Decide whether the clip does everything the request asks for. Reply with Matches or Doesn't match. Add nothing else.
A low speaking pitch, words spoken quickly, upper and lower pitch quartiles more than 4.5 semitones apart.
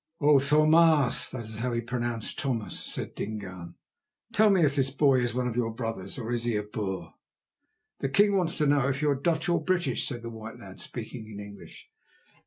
Matches